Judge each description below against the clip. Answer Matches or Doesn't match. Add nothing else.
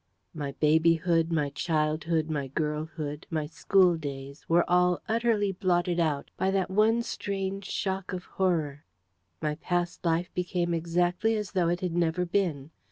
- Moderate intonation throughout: Matches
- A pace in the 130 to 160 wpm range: Matches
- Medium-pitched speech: Matches